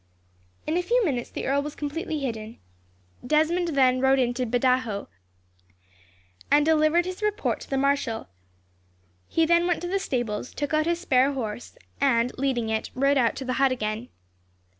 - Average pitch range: Yes, average, 4.4 semitones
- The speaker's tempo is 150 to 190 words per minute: Yes, average, 165 wpm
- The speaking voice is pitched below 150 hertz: No, very high, 275 Hz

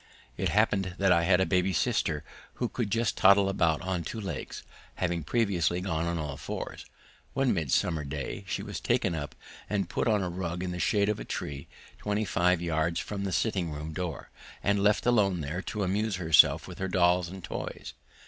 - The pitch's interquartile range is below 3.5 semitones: Yes, average, 3.1 semitones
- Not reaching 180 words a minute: No, average, 195 wpm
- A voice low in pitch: Yes, very low, 90 Hz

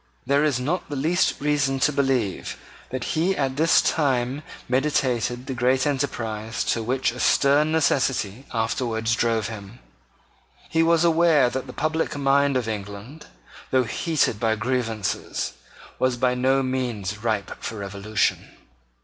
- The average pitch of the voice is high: No, low, 130 Hz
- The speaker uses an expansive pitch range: No, average, 3.9 semitones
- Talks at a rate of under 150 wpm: Yes, average, 140 wpm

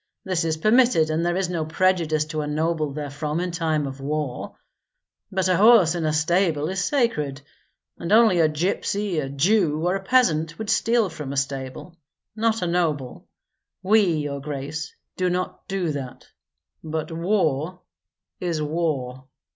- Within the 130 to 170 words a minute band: Yes, average, 160 wpm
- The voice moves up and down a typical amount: Yes, average, 3.7 semitones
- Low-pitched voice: No, medium, 165 Hz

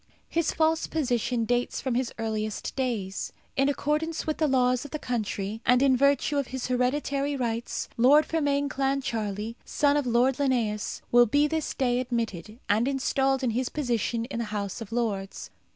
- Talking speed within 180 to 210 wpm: No, average, 170 wpm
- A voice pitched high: Yes, very high, 250 Hz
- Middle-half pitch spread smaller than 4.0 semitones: Yes, average, 3.6 semitones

